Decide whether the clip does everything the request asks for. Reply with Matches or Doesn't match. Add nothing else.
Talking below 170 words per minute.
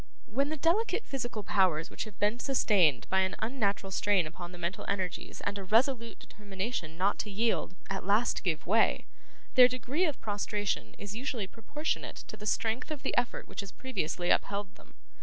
Doesn't match